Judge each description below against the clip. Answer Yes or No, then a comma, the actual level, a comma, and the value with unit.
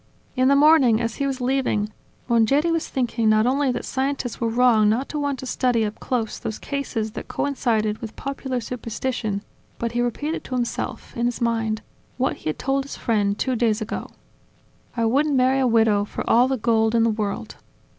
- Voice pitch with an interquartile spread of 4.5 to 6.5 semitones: No, average, 3.2 semitones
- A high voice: Yes, high, 240 Hz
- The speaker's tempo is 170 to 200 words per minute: Yes, average, 195 wpm